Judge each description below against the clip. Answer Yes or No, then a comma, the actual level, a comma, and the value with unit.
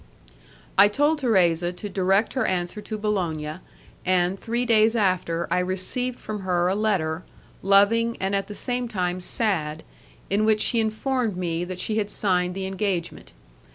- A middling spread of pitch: Yes, average, 3.3 semitones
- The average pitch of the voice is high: Yes, high, 195 Hz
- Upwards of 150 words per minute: Yes, average, 160 wpm